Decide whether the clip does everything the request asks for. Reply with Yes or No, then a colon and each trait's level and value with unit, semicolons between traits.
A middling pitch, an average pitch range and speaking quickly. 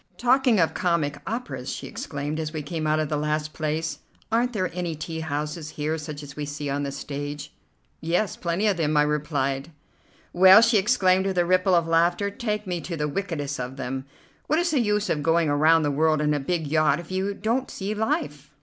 Yes: medium, 160 Hz; average, 4.2 semitones; fast, 215 wpm